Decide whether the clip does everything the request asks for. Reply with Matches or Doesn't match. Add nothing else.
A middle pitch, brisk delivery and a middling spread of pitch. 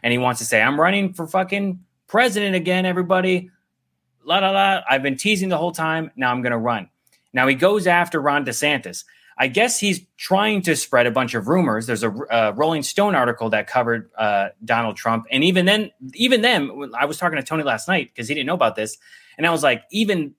Doesn't match